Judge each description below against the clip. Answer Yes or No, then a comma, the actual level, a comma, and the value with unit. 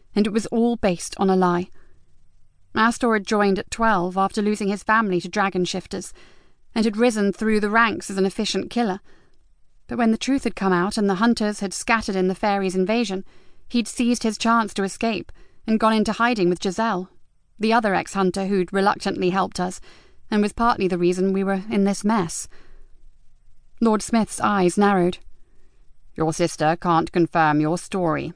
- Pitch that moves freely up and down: No, average, 3.5 semitones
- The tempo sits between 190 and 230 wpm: No, average, 180 wpm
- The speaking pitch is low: No, high, 200 Hz